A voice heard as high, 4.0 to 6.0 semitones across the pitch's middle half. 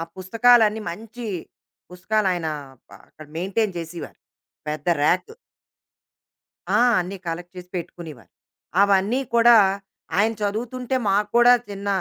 Yes: high, 195 Hz; average, 4.3 semitones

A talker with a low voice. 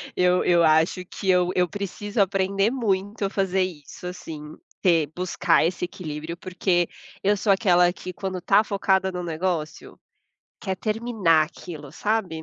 No: medium, 185 Hz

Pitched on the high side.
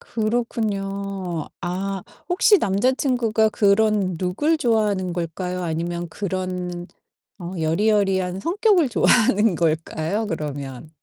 Yes: high, 195 Hz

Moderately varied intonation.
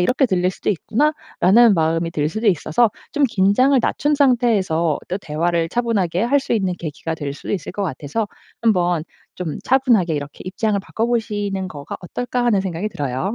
No: wide, 5.9 semitones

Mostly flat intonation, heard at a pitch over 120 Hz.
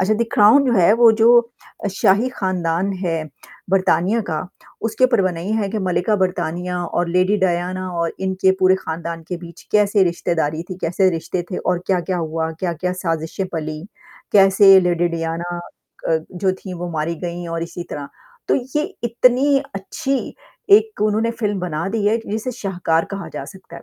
No: average, 3.4 semitones; medium, 185 Hz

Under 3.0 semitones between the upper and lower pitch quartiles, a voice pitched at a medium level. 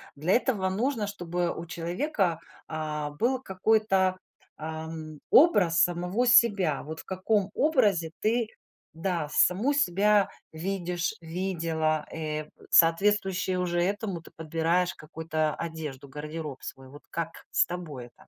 No: average, 3.8 semitones; medium, 175 Hz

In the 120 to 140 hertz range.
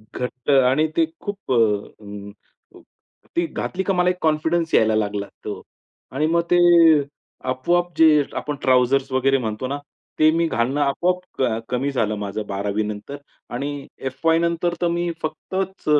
Yes: low, 135 Hz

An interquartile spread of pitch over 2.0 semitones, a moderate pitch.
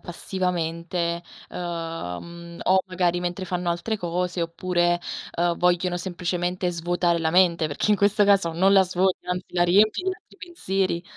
No: narrow, 1.6 semitones; medium, 180 Hz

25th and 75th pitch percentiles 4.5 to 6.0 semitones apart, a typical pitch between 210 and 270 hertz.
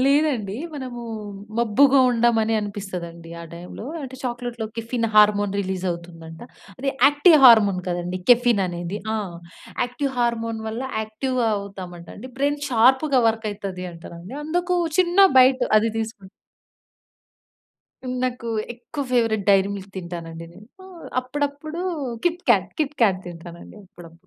Yes: wide, 5.4 semitones; high, 225 Hz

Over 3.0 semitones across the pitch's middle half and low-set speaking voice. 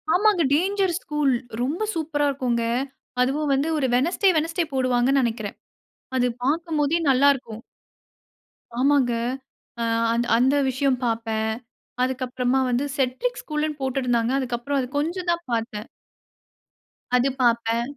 No: average, 3.9 semitones; very high, 270 Hz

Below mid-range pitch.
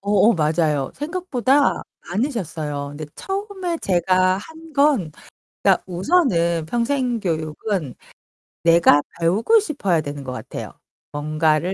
No: medium, 185 Hz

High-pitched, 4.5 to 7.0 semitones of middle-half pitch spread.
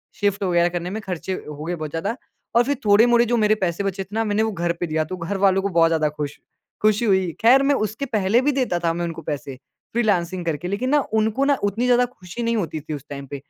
Yes: high, 195 Hz; average, 4.9 semitones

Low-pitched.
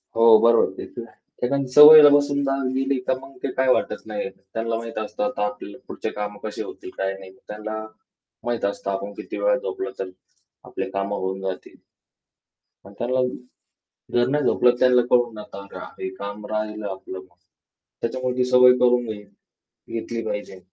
Yes: low, 115 Hz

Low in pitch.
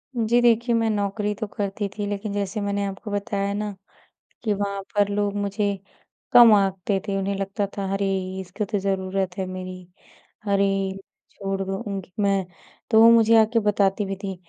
No: high, 200 Hz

